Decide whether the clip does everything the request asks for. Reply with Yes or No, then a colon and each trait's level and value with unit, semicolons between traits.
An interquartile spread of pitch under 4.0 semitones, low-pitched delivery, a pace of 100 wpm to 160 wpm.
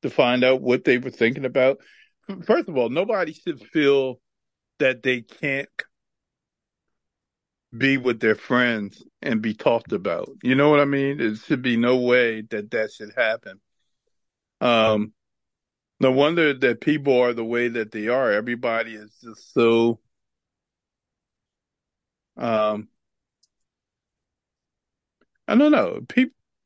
Yes: average, 3.6 semitones; low, 125 Hz; slow, 135 wpm